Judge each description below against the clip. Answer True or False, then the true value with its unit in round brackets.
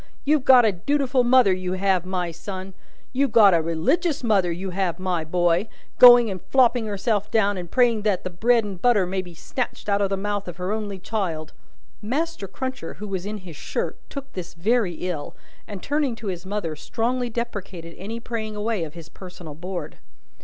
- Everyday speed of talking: True (195 wpm)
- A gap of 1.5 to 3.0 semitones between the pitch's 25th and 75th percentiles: False (4.5 semitones)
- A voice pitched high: True (200 Hz)